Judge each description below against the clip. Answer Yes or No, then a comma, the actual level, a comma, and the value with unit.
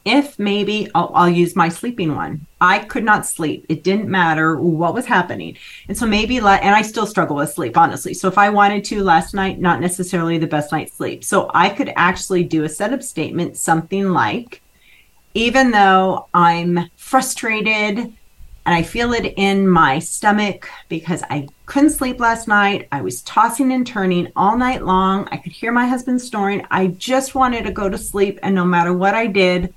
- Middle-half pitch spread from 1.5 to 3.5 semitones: No, average, 4.0 semitones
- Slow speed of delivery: No, average, 195 wpm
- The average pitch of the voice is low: No, high, 195 Hz